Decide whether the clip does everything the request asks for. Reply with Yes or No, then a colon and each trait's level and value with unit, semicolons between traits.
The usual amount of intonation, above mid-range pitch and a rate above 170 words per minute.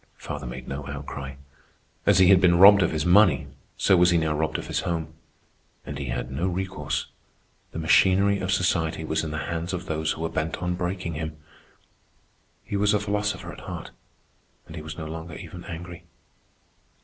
No: average, 3.0 semitones; very low, 85 Hz; average, 190 wpm